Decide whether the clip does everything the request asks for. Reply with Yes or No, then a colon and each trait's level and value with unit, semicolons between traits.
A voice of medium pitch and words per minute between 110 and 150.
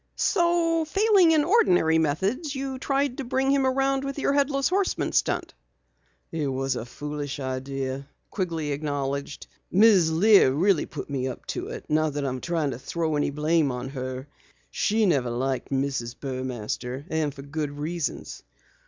No: medium, 155 Hz; average, 160 wpm